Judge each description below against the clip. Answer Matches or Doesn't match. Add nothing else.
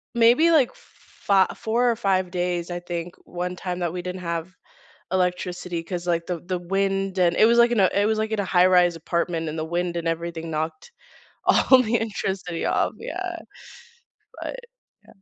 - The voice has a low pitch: Doesn't match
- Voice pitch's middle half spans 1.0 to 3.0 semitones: Matches